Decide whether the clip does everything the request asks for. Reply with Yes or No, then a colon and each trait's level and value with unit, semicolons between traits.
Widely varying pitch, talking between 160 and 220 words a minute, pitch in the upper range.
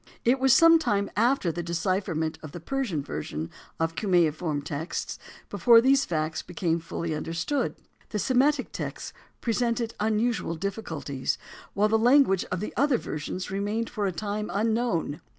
No: wide, 6.2 semitones; average, 150 wpm; high, 200 Hz